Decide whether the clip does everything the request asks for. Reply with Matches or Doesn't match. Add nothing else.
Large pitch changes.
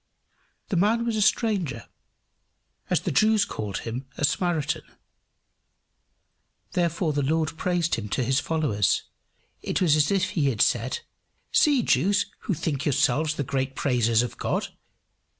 Matches